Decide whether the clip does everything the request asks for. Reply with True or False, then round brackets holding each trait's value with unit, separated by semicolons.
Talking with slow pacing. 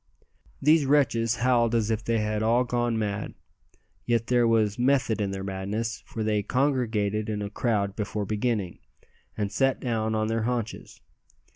False (160 wpm)